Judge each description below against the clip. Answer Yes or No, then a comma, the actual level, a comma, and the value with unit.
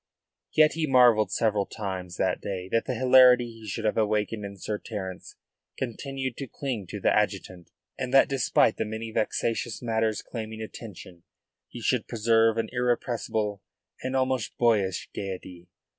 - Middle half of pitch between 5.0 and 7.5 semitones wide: No, average, 3.2 semitones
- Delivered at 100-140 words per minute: No, average, 155 wpm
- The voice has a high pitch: No, low, 110 Hz